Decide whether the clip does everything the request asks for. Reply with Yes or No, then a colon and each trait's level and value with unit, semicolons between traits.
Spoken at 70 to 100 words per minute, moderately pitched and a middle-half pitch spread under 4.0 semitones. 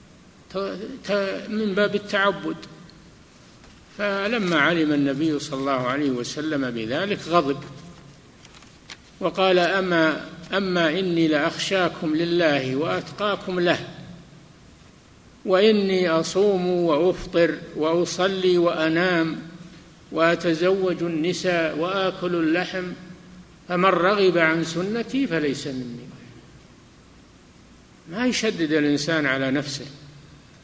Yes: average, 80 wpm; medium, 170 Hz; average, 2.9 semitones